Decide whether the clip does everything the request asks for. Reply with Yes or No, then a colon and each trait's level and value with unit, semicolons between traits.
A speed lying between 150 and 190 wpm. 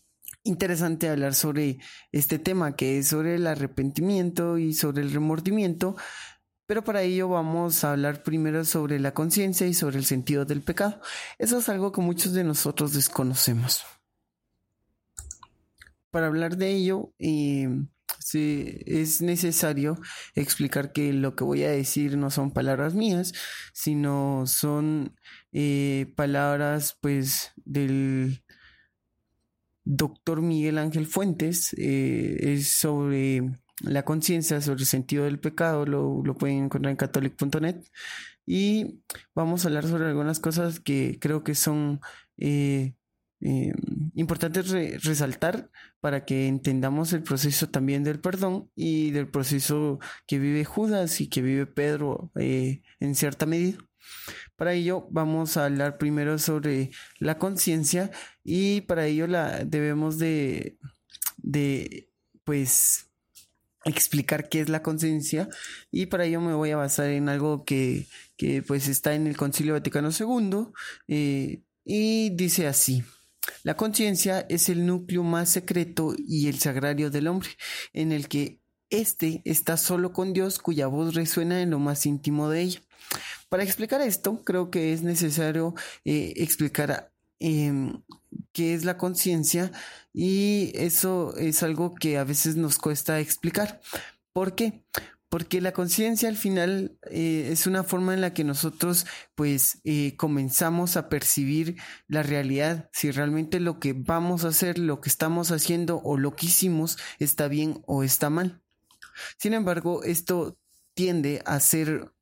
No: average, 140 wpm